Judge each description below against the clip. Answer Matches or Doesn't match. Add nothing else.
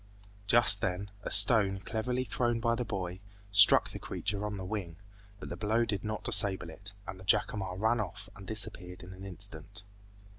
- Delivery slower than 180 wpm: Doesn't match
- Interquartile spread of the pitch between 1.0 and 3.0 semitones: Matches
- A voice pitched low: Matches